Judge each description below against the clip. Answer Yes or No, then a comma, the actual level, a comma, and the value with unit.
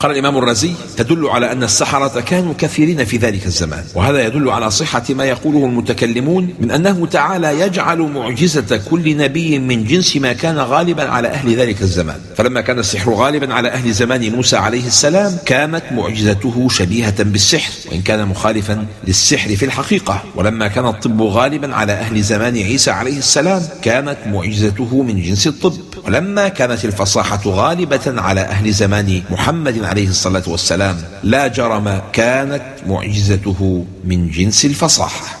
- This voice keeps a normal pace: Yes, average, 150 wpm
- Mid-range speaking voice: No, low, 120 Hz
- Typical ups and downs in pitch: No, wide, 5.7 semitones